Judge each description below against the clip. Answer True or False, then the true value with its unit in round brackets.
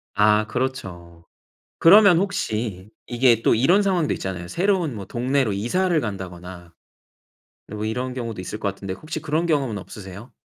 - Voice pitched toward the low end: True (115 Hz)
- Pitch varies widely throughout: True (7.9 semitones)